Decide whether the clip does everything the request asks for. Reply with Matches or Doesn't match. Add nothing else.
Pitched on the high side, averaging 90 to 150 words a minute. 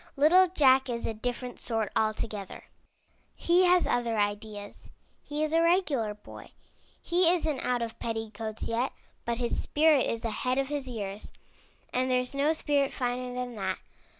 Doesn't match